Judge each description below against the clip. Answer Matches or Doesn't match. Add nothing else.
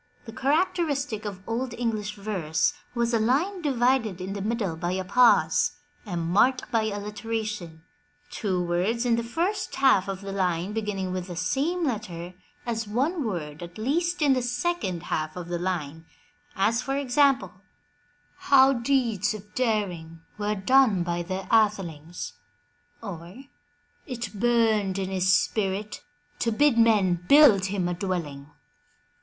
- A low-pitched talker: Doesn't match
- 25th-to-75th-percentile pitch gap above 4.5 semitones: Matches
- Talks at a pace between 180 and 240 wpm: Doesn't match